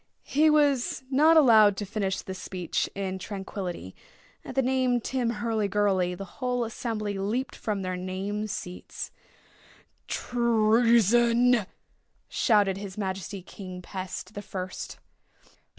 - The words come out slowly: Yes, slow, 120 wpm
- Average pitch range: Yes, average, 3.9 semitones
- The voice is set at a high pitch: Yes, high, 210 Hz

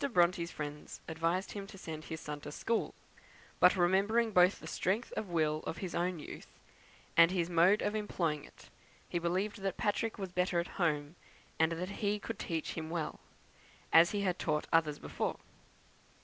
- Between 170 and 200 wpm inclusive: Yes, average, 180 wpm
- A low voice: No, medium, 175 Hz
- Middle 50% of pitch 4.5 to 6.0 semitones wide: No, average, 3.2 semitones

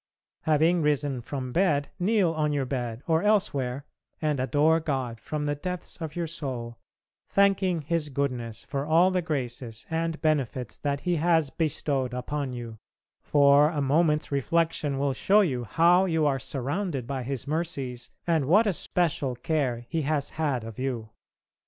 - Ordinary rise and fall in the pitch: Yes, average, 4.0 semitones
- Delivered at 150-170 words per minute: Yes, average, 160 wpm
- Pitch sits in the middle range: Yes, medium, 145 Hz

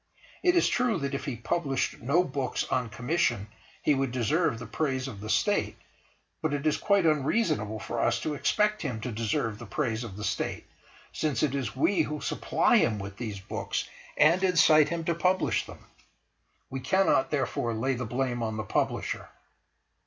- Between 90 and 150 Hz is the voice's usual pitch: Yes, low, 135 Hz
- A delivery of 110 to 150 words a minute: No, average, 180 wpm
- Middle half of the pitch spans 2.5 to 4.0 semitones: No, wide, 5.6 semitones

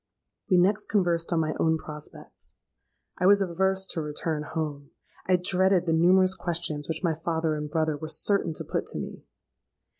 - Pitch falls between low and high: Yes, medium, 165 Hz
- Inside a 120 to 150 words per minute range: No, average, 175 wpm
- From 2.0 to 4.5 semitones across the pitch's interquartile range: Yes, average, 2.9 semitones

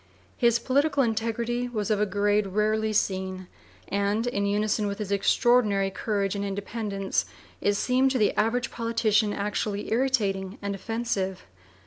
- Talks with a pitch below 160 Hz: No, high, 210 Hz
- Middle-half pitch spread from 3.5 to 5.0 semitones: No, narrow, 2.5 semitones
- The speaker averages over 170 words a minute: No, average, 140 wpm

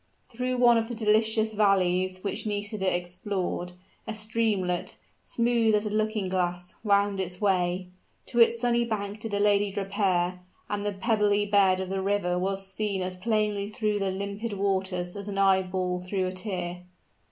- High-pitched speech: Yes, high, 200 Hz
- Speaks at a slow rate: No, average, 165 wpm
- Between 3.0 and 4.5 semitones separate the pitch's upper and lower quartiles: No, narrow, 2.5 semitones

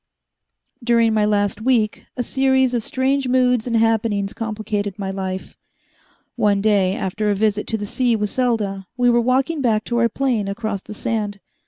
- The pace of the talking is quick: No, average, 175 wpm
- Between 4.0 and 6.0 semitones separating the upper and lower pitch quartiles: No, average, 3.2 semitones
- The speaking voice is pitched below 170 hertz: No, high, 220 Hz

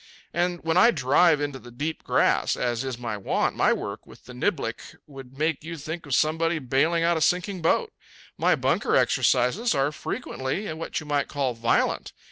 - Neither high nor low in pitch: Yes, medium, 150 Hz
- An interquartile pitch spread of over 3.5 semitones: Yes, average, 4.0 semitones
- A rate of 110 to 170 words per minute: No, average, 185 wpm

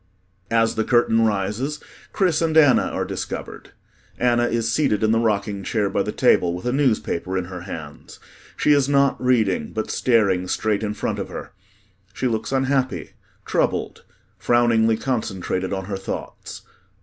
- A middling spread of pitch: Yes, average, 4.4 semitones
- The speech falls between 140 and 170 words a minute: Yes, average, 160 wpm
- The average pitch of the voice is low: Yes, low, 115 Hz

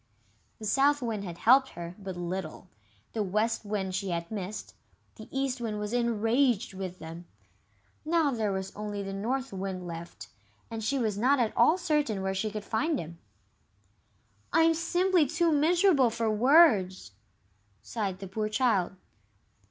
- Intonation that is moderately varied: No, wide, 5.9 semitones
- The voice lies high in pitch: Yes, high, 215 Hz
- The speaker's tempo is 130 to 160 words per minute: Yes, average, 155 wpm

